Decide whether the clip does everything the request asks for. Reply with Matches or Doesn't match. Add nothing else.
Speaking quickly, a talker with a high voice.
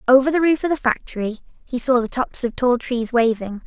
Matches